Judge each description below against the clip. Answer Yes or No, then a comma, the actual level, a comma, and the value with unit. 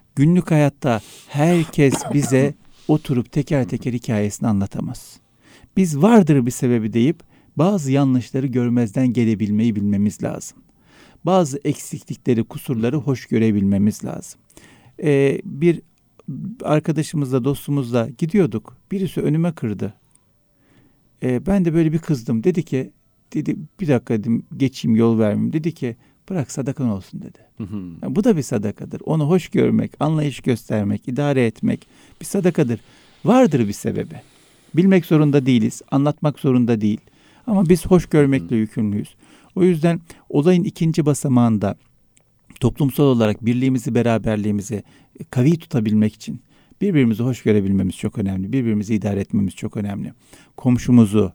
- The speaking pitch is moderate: No, low, 130 Hz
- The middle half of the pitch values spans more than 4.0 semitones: Yes, wide, 5.4 semitones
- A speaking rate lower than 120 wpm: No, average, 125 wpm